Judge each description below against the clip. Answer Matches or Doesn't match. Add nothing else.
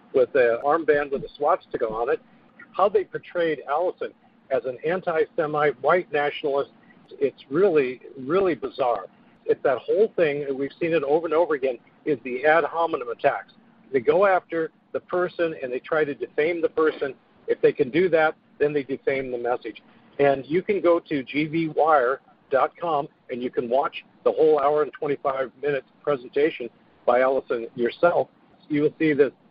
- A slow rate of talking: Doesn't match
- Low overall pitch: Doesn't match